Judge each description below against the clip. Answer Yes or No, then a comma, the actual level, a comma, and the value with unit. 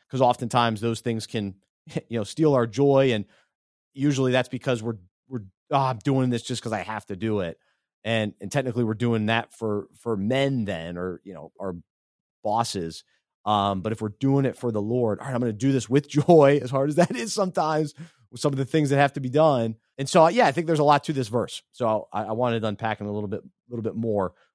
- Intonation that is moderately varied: Yes, average, 4.1 semitones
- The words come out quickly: Yes, fast, 245 wpm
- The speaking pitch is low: Yes, low, 120 Hz